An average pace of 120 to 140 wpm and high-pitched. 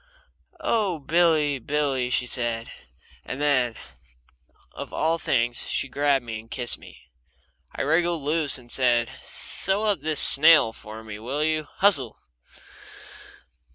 No: slow, 135 wpm; medium, 140 Hz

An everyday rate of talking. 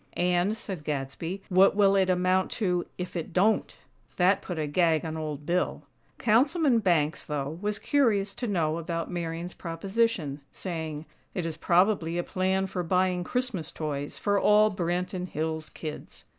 Yes: average, 155 wpm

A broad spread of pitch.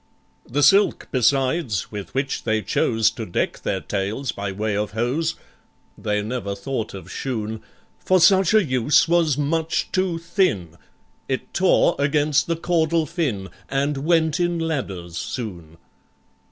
Yes: wide, 7.5 semitones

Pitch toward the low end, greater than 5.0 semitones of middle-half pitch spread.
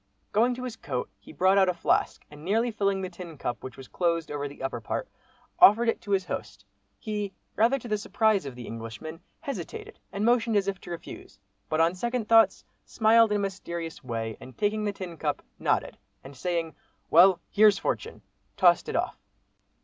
No: high, 190 Hz; wide, 5.5 semitones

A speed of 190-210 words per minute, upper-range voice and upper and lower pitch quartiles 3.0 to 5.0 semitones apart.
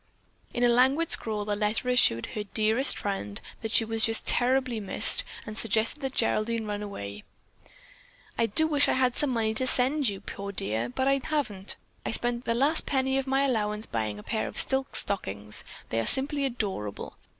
Yes: average, 195 wpm; high, 225 Hz; average, 4.4 semitones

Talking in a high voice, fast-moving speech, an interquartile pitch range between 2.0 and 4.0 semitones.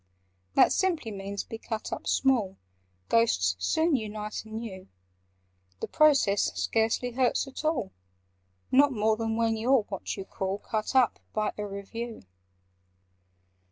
No: high, 225 Hz; slow, 135 wpm; average, 3.7 semitones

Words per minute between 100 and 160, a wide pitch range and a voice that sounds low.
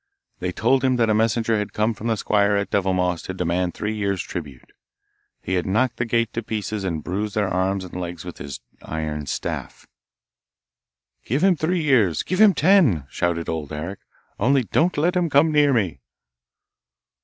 No: average, 180 wpm; wide, 5.9 semitones; low, 105 Hz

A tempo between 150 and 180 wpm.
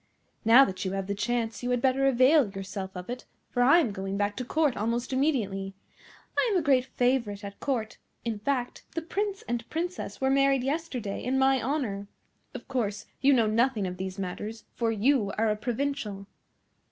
No: average, 190 wpm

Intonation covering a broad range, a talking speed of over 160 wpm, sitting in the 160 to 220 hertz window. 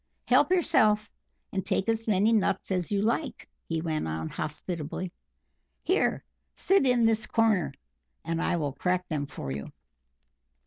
No: wide, 5.9 semitones; average, 145 wpm; medium, 185 Hz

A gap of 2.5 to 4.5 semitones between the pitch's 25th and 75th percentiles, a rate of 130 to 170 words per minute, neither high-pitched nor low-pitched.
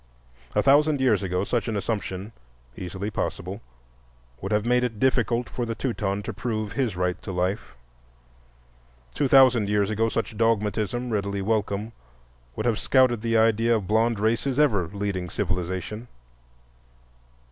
No: average, 3.0 semitones; average, 145 wpm; low, 110 Hz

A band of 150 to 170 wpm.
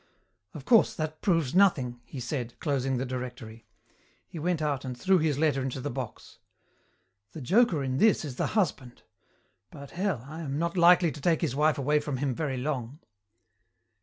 No: average, 180 wpm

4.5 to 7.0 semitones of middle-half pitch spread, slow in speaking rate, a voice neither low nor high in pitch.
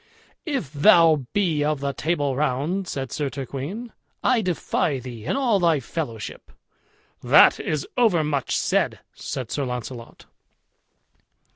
Yes: average, 4.9 semitones; slow, 125 wpm; medium, 150 Hz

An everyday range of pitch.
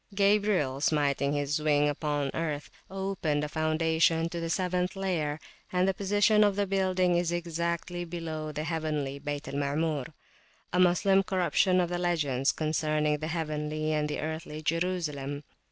Yes: average, 3.2 semitones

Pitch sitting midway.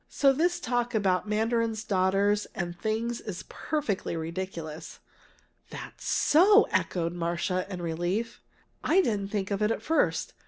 No: high, 205 Hz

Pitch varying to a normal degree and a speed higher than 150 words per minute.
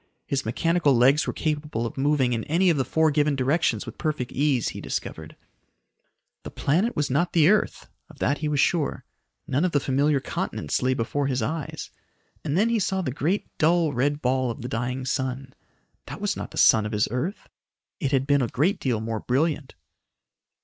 Yes: average, 3.7 semitones; average, 195 wpm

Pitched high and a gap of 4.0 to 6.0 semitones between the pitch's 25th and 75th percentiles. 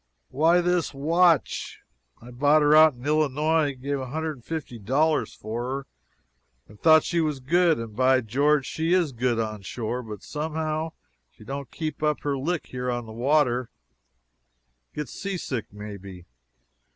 No: medium, 140 Hz; average, 4.5 semitones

